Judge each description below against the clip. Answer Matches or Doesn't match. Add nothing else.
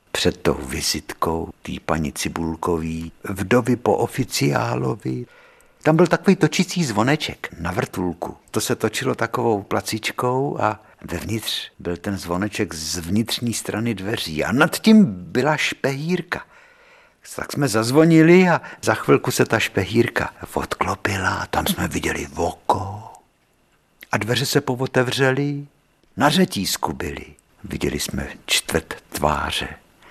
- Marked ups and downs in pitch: Matches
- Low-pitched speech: Matches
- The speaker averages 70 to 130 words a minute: Matches